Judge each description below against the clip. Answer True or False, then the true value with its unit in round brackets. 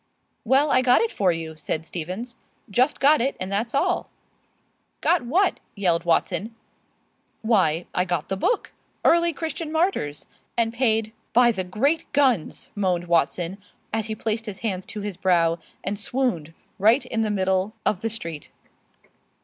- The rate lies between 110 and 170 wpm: True (160 wpm)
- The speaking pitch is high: True (215 Hz)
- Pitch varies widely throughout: True (5.8 semitones)